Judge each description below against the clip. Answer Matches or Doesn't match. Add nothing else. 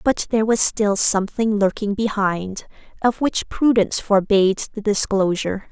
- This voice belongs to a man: Doesn't match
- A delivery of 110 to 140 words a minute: Matches